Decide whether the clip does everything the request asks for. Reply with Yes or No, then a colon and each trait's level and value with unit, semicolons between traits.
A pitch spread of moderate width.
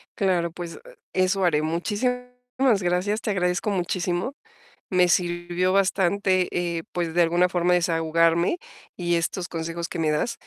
No: narrow, 1.7 semitones